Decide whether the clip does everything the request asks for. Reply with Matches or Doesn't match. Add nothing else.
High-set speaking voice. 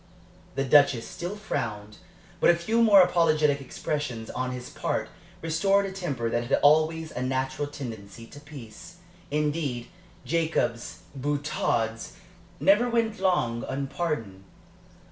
Doesn't match